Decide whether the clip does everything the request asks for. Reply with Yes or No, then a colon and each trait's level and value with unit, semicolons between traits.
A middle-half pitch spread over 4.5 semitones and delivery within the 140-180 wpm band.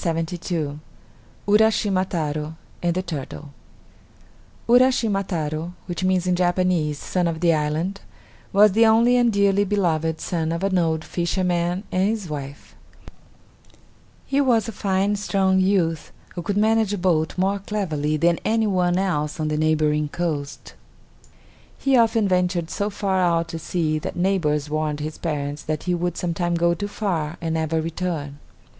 No: average, 3.8 semitones; average, 150 wpm